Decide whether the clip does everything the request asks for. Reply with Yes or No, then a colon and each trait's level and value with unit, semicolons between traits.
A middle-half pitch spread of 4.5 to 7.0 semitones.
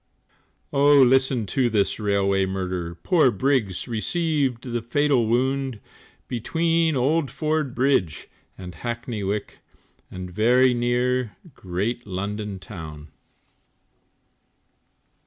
Yes: average, 5.3 semitones